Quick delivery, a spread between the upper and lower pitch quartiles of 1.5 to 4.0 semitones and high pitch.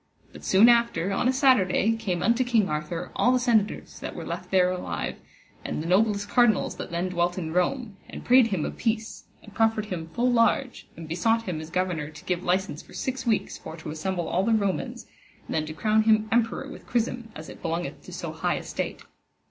No: fast, 210 wpm; average, 4.8 semitones; high, 205 Hz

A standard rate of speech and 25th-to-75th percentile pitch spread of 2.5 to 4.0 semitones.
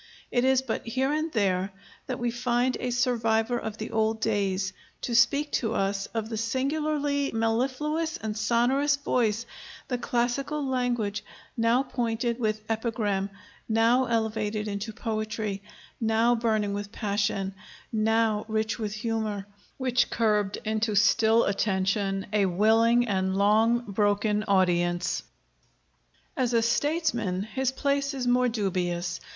No: slow, 130 wpm; average, 2.9 semitones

